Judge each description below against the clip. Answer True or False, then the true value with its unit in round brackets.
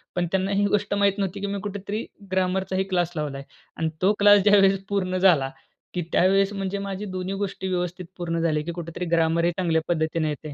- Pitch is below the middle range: False (185 Hz)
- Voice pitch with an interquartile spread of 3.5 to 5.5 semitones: False (2.8 semitones)